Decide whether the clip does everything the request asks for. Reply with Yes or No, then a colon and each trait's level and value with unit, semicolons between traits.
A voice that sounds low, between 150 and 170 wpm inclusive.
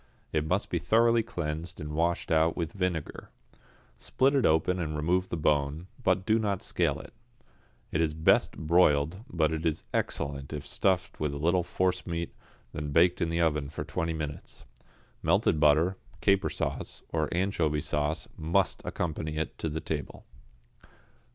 Yes: very low, 80 Hz; average, 155 wpm